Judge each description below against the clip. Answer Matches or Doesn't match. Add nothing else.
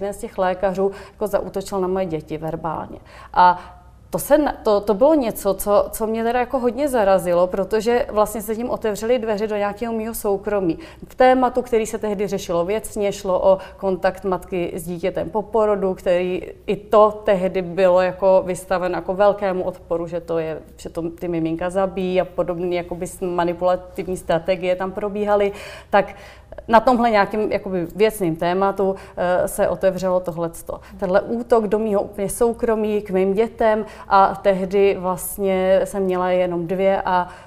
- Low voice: Doesn't match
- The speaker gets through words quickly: Doesn't match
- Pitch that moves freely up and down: Doesn't match